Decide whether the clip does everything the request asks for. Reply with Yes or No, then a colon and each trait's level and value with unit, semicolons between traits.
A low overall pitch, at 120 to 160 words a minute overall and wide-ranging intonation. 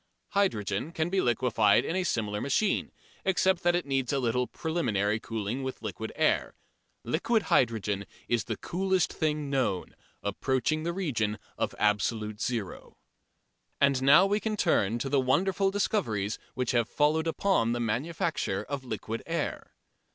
Yes: low, 130 Hz; average, 150 wpm; wide, 7.4 semitones